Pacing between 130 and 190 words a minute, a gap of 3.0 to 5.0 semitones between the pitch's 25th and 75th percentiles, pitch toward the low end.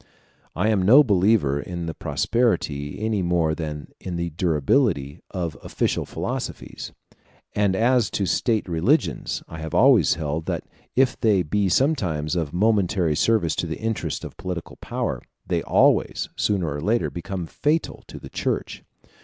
No: average, 155 wpm; wide, 5.4 semitones; very low, 90 Hz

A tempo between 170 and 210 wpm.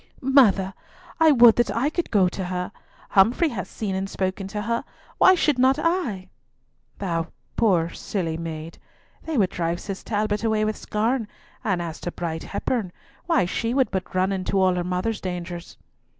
Yes: average, 175 wpm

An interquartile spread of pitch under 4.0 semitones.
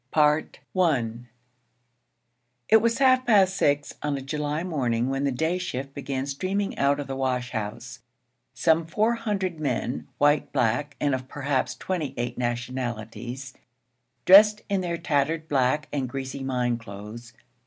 No: average, 4.6 semitones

